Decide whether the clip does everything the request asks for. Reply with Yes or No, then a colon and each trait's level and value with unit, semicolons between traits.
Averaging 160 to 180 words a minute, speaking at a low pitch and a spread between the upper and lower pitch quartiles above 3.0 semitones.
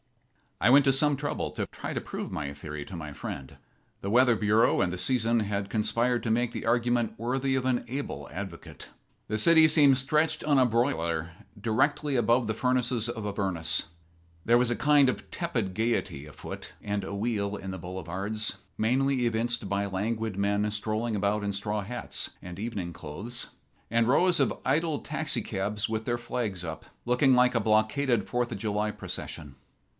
Yes: average, 175 wpm; low, 115 Hz; average, 3.9 semitones